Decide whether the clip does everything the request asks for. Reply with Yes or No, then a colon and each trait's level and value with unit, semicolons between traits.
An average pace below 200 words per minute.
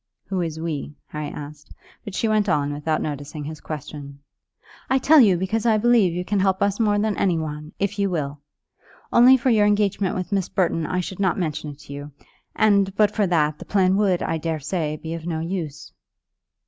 No: fast, 205 wpm